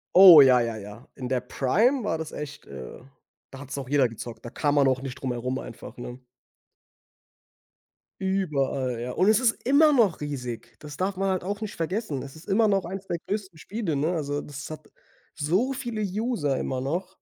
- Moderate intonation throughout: No, wide, 6.9 semitones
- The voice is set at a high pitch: No, medium, 150 Hz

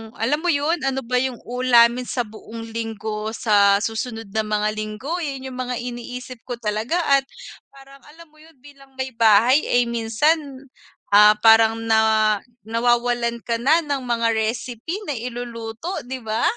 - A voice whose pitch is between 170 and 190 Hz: No, high, 235 Hz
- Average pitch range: Yes, average, 3.0 semitones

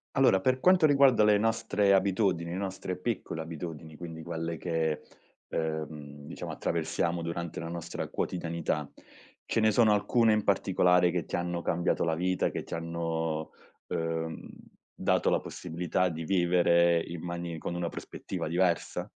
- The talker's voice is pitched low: Yes, very low, 85 Hz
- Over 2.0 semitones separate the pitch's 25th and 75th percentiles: Yes, average, 2.7 semitones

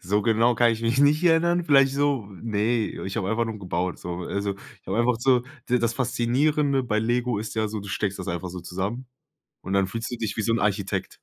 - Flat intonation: No, average, 3.7 semitones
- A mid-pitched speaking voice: No, low, 115 Hz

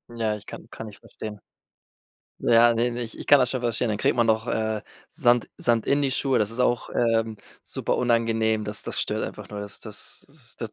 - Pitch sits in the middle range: No, low, 115 Hz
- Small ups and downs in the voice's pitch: Yes, narrow, 1.7 semitones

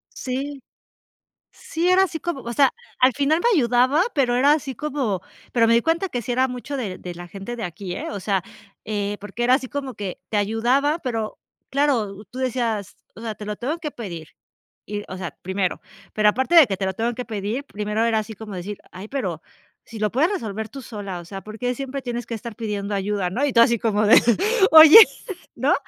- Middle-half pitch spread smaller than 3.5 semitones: No, average, 4.5 semitones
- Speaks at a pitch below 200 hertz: No, high, 230 Hz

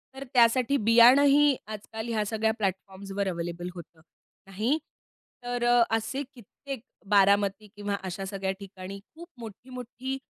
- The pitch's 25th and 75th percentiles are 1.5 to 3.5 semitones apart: No, average, 4.0 semitones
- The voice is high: Yes, high, 220 Hz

